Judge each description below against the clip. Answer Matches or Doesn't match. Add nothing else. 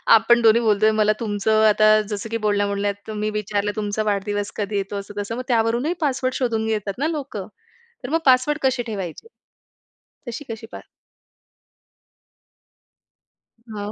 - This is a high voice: Matches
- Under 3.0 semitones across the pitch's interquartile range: Matches